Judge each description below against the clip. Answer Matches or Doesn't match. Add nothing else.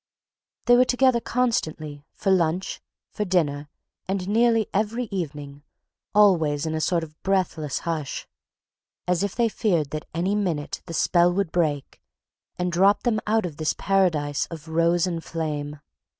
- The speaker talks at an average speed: Matches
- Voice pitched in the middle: Matches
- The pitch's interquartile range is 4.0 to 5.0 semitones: Matches